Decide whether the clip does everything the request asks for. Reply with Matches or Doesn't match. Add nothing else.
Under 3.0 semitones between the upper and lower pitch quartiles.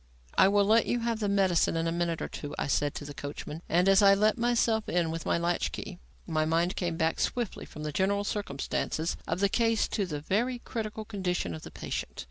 Doesn't match